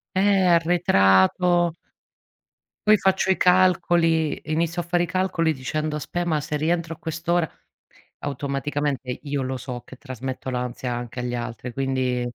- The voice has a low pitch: No, medium, 150 Hz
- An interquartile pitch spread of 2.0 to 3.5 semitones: No, average, 5.2 semitones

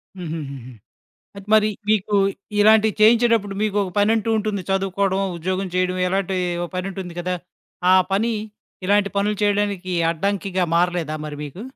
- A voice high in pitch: Yes, high, 195 Hz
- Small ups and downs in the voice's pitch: Yes, narrow, 2.2 semitones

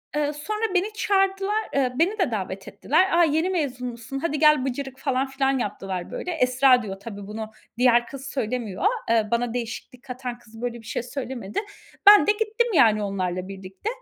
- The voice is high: Yes, very high, 255 Hz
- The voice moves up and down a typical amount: No, wide, 5.9 semitones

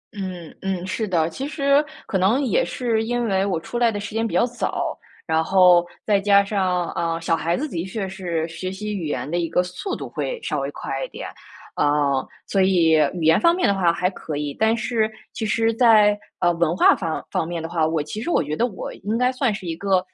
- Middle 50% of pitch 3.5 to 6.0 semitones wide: Yes, average, 4.8 semitones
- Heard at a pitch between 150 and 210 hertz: Yes, high, 190 Hz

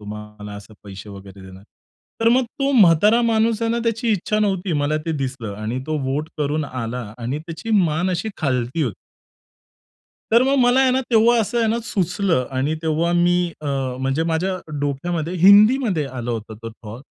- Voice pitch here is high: No, medium, 160 Hz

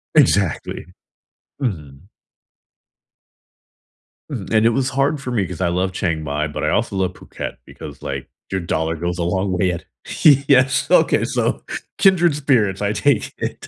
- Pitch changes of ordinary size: No, wide, 7.3 semitones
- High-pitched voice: No, very low, 95 Hz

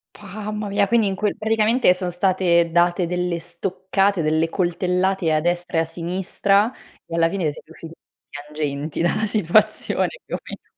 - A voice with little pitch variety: No, average, 3.1 semitones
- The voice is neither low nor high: Yes, medium, 180 Hz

